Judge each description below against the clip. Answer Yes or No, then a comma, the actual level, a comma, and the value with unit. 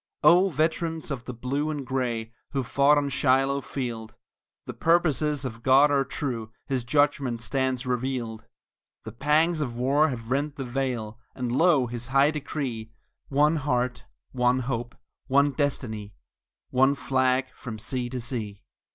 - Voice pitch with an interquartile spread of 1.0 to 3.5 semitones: Yes, average, 3.0 semitones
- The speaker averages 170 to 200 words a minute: No, average, 150 wpm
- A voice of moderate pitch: No, low, 130 Hz